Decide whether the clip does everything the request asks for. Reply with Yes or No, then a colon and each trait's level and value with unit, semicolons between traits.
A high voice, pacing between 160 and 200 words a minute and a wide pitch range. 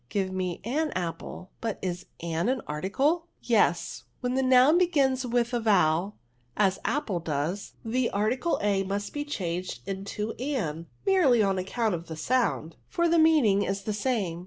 Yes: high, 210 Hz; average, 170 wpm; wide, 5.9 semitones